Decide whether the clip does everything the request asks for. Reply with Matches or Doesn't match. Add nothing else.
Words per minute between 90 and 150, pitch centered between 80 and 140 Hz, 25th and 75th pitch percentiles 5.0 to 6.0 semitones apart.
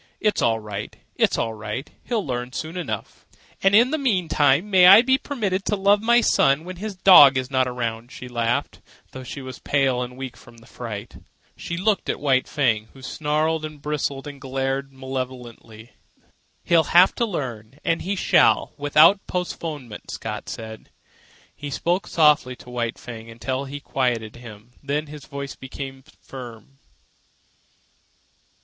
Doesn't match